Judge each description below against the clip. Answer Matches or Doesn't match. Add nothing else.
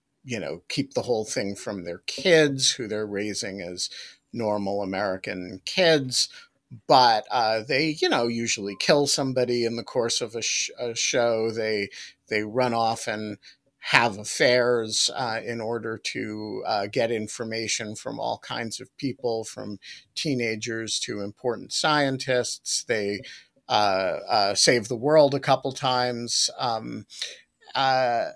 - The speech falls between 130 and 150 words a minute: Matches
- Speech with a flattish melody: Doesn't match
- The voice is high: Doesn't match